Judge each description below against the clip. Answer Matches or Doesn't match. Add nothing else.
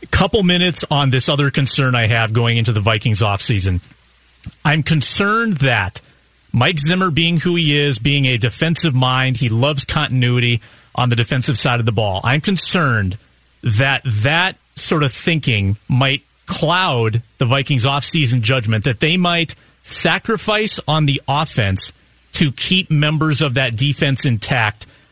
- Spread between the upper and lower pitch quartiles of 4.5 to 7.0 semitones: Matches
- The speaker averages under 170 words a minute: Matches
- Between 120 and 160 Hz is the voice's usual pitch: Matches